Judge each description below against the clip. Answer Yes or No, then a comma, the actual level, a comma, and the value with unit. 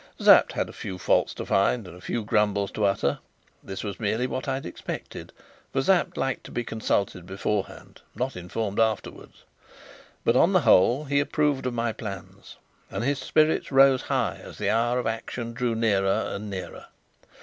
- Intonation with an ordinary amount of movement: Yes, average, 4.4 semitones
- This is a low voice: Yes, low, 115 Hz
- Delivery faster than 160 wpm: Yes, average, 180 wpm